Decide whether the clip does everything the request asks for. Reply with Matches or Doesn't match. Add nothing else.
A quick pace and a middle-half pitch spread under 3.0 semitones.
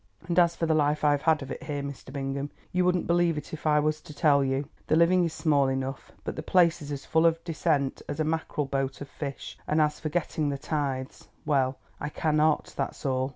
Matches